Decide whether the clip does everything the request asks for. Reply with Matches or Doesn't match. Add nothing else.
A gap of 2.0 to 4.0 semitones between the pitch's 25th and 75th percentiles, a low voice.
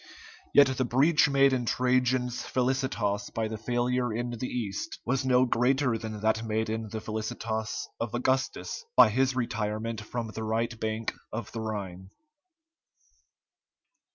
Matches